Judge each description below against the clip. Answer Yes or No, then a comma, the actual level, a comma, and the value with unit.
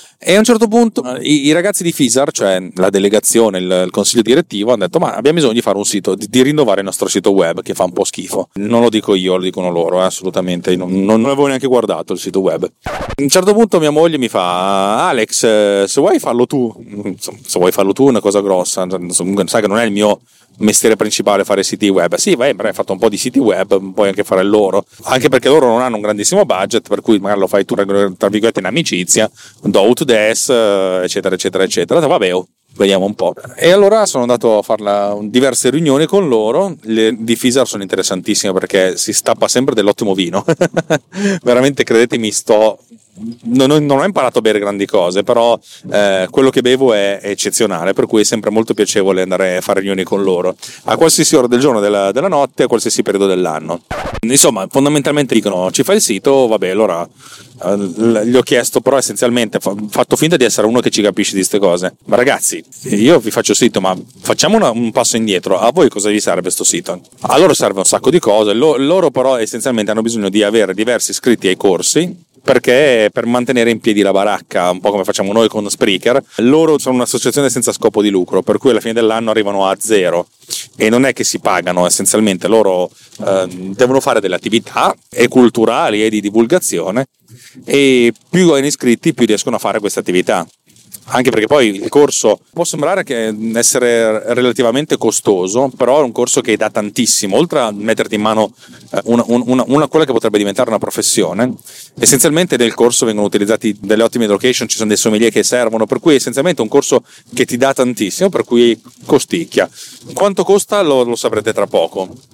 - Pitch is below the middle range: Yes, low, 115 Hz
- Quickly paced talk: Yes, fast, 205 wpm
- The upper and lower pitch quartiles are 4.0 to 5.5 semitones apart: Yes, average, 4.9 semitones